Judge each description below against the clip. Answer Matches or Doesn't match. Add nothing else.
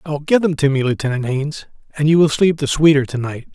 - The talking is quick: Matches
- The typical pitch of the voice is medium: Matches